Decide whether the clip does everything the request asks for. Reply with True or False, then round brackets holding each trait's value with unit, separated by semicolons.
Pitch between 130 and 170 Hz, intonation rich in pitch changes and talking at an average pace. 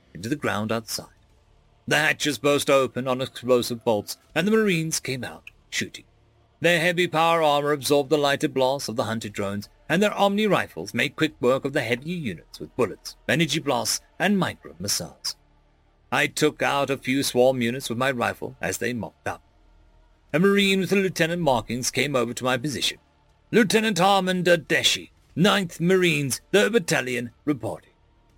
True (140 Hz; 6.0 semitones; 170 wpm)